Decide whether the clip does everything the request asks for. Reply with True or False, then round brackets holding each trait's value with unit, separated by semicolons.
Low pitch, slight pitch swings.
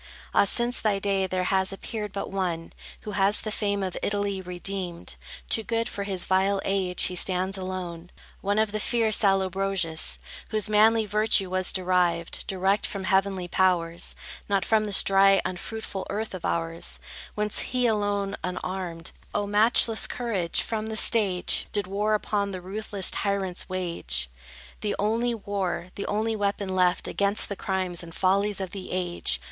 False (195 Hz; 2.1 semitones)